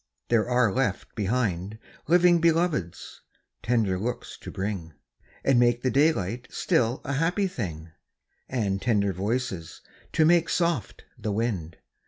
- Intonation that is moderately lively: No, wide, 6.3 semitones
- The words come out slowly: Yes, slow, 130 wpm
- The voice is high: No, low, 120 Hz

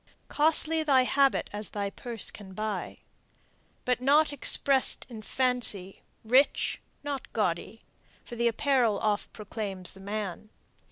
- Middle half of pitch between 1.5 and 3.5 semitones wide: No, average, 4.7 semitones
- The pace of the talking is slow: Yes, slow, 125 wpm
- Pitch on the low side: No, high, 230 Hz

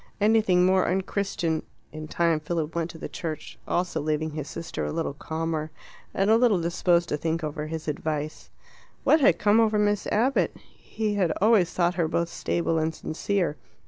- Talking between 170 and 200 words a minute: Yes, average, 180 wpm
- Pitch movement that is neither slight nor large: Yes, average, 3.9 semitones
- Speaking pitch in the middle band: Yes, medium, 170 Hz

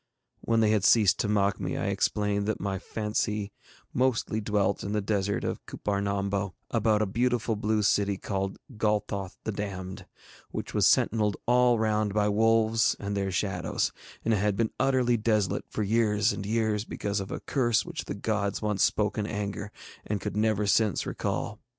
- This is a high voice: No, low, 105 Hz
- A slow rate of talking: No, average, 175 wpm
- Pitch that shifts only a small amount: Yes, narrow, 1.6 semitones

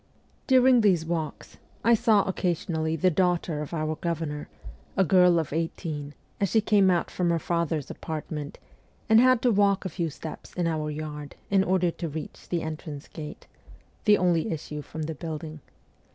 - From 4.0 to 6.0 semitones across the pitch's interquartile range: No, average, 3.5 semitones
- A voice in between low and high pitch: Yes, medium, 165 Hz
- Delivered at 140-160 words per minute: No, average, 170 wpm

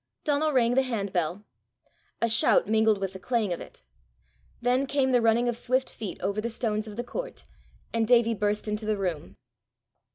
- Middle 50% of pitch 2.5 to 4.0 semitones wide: Yes, average, 3.1 semitones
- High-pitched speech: Yes, high, 225 Hz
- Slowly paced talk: No, average, 185 wpm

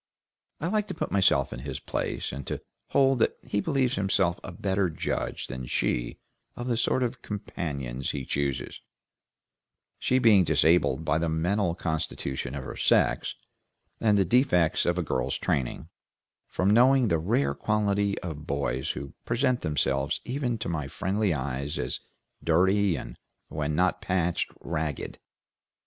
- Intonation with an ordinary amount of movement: No, wide, 6.8 semitones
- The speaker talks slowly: No, average, 155 wpm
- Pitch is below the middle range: Yes, very low, 85 Hz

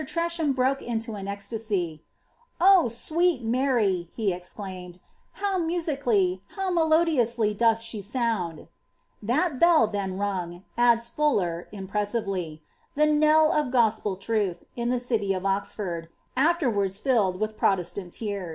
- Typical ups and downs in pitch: No, wide, 6.0 semitones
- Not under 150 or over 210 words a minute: No, slow, 135 wpm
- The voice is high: Yes, high, 225 Hz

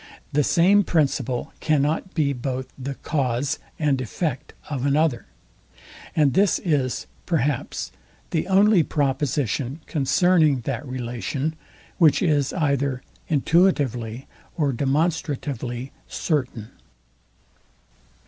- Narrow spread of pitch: No, average, 3.6 semitones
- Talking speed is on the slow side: Yes, slow, 95 wpm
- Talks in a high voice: No, medium, 140 Hz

